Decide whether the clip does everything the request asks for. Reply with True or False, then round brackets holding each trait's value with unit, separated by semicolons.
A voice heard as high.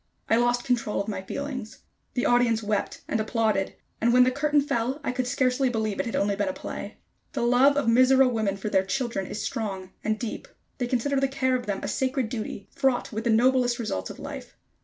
True (240 Hz)